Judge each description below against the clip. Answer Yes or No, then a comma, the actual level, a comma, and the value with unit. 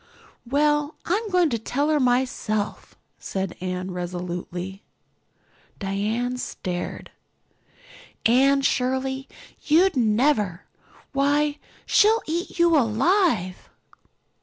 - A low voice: No, very high, 255 Hz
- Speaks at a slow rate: Yes, slow, 90 wpm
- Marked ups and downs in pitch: Yes, wide, 7.1 semitones